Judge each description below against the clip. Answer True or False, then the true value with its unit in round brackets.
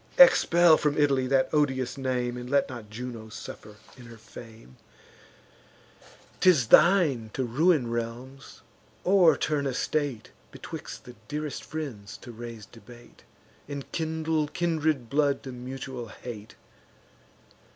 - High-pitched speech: False (130 Hz)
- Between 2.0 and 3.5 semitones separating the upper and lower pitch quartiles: False (4.2 semitones)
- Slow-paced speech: True (120 wpm)